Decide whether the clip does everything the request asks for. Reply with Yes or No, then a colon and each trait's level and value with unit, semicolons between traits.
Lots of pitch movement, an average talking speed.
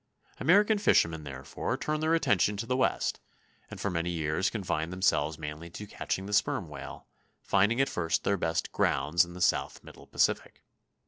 No: average, 4.8 semitones; average, 175 wpm